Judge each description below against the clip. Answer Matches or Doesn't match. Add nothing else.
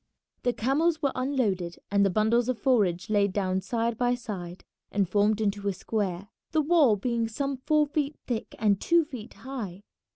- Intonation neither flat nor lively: Matches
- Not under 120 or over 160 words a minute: Doesn't match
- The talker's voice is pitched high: Matches